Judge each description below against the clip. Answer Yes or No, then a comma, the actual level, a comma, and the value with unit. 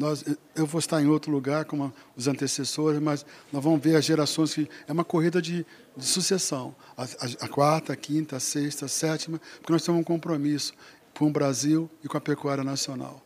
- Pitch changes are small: Yes, narrow, 2.0 semitones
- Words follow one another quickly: Yes, fast, 210 wpm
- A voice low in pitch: No, medium, 150 Hz